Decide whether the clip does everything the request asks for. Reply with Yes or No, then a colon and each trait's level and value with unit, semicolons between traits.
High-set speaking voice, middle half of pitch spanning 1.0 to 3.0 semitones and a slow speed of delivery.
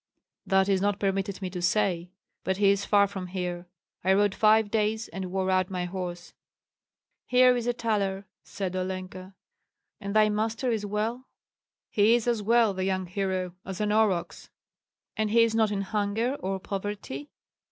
No: high, 200 Hz; narrow, 2.4 semitones; average, 175 wpm